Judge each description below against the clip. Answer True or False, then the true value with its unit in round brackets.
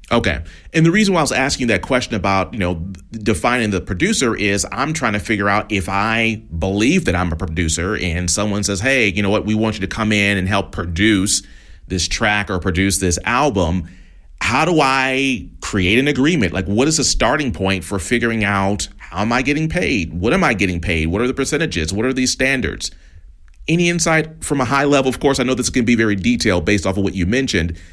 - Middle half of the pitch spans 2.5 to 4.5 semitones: False (5.4 semitones)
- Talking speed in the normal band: False (225 wpm)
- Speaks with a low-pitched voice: True (105 Hz)